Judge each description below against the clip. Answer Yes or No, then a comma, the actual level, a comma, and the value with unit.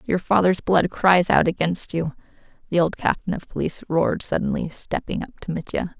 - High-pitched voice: No, medium, 170 Hz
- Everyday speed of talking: Yes, average, 180 wpm